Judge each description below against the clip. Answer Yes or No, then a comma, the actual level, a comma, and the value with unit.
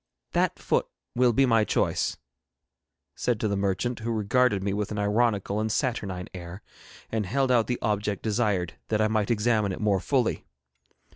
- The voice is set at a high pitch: No, low, 105 Hz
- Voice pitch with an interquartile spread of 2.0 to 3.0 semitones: Yes, average, 2.7 semitones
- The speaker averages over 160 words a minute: Yes, average, 170 wpm